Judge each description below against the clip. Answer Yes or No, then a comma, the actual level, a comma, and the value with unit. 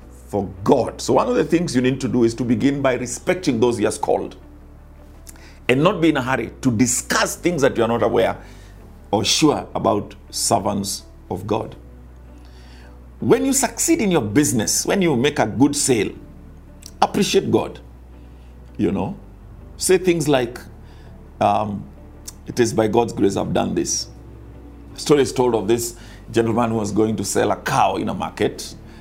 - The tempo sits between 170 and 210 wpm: Yes, average, 175 wpm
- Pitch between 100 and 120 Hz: Yes, low, 105 Hz